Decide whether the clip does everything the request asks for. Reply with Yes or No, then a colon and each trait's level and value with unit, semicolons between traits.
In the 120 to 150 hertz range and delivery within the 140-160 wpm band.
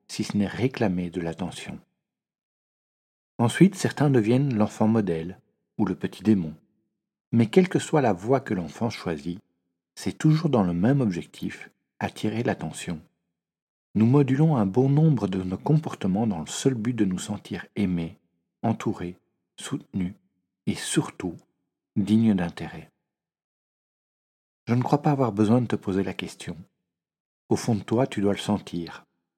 No: low, 105 Hz; average, 150 wpm